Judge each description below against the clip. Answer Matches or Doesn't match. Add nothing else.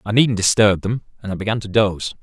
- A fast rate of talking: Matches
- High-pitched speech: Doesn't match